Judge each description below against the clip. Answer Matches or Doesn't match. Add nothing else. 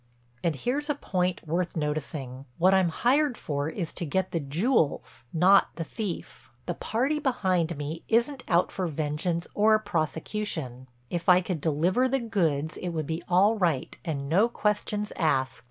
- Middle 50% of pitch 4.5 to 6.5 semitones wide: Matches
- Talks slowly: Doesn't match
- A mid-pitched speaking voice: Matches